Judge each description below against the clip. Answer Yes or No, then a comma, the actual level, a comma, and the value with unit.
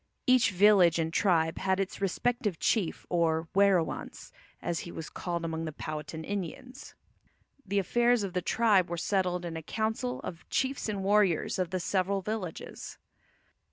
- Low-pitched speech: No, medium, 185 Hz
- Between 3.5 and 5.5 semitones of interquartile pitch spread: Yes, average, 3.8 semitones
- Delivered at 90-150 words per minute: No, average, 160 wpm